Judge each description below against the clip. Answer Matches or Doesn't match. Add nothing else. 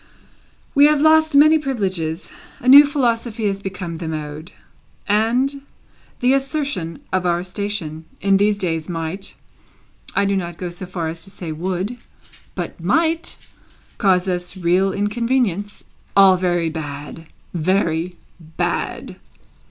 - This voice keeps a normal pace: Doesn't match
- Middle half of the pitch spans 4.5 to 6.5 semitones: Matches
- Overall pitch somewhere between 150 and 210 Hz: Matches